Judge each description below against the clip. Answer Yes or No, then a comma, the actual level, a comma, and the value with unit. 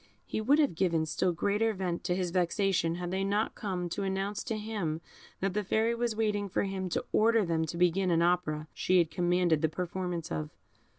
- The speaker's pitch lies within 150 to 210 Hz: Yes, medium, 185 Hz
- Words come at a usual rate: No, fast, 210 wpm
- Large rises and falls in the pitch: No, average, 3.2 semitones